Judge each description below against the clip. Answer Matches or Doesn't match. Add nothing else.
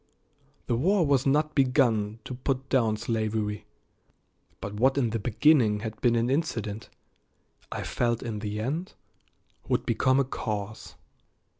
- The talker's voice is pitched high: Doesn't match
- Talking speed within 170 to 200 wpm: Doesn't match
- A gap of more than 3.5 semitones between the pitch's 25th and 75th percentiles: Matches